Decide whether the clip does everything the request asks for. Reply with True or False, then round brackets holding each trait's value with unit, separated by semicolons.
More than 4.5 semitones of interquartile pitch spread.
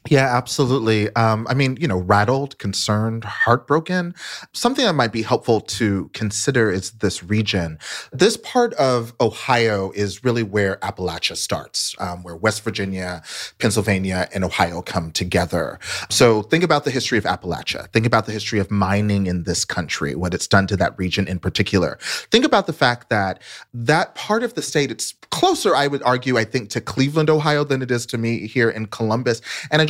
True (5.0 semitones)